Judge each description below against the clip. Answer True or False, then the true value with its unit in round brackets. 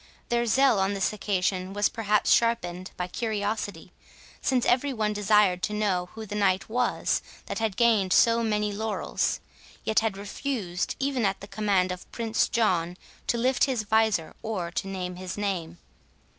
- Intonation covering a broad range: False (3.2 semitones)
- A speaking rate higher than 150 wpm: True (165 wpm)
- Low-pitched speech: False (210 Hz)